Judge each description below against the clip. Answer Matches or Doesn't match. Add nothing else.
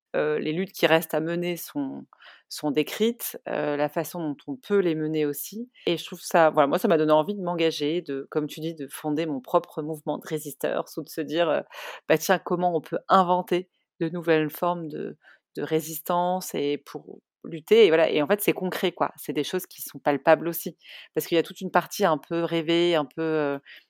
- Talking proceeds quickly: Matches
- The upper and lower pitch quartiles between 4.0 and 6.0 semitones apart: Doesn't match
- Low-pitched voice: Doesn't match